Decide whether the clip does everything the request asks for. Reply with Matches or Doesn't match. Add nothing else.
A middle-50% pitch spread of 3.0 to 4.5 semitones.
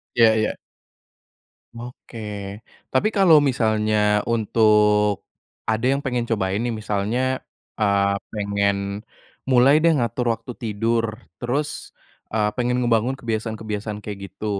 Doesn't match